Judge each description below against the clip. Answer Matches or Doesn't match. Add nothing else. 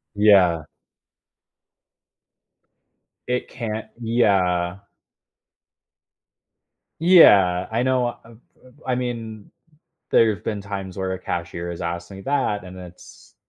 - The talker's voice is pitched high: Doesn't match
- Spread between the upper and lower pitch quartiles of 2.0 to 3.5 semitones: Doesn't match